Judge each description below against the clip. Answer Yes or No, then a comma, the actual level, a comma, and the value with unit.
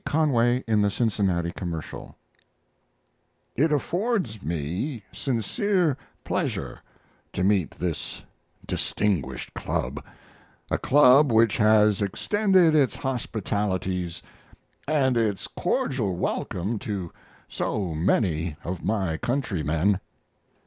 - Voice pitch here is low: Yes, low, 105 Hz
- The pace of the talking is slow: Yes, slow, 95 wpm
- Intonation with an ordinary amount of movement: No, wide, 6.6 semitones